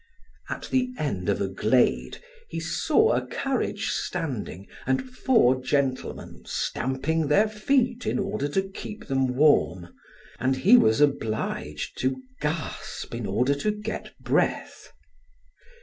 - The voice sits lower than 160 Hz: Yes, medium, 140 Hz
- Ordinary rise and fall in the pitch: No, wide, 8.9 semitones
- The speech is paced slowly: Yes, slow, 130 wpm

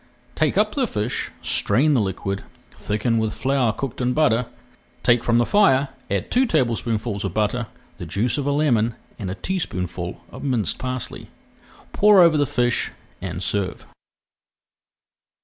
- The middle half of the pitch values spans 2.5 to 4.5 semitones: No, average, 5.1 semitones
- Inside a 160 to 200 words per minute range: No, average, 150 wpm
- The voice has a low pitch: Yes, low, 120 Hz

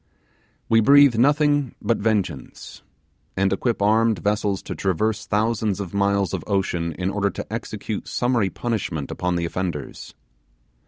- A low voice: Yes, low, 100 Hz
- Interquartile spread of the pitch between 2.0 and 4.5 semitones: Yes, average, 3.3 semitones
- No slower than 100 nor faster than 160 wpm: Yes, average, 140 wpm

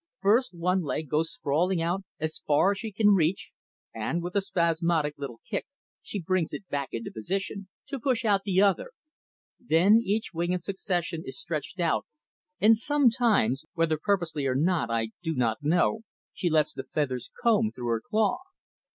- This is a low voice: No, medium, 175 Hz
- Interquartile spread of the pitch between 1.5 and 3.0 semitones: No, average, 4.8 semitones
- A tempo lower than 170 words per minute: No, average, 175 wpm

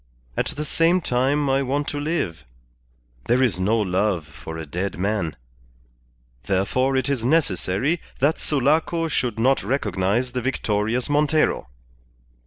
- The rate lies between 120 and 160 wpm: Yes, slow, 135 wpm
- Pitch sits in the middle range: No, low, 125 Hz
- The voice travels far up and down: Yes, wide, 6.7 semitones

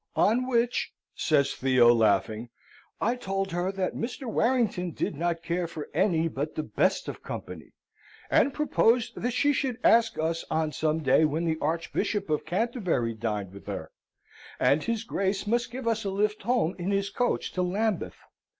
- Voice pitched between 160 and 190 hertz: Yes, medium, 185 Hz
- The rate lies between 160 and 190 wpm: Yes, average, 170 wpm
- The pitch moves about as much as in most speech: No, wide, 6.6 semitones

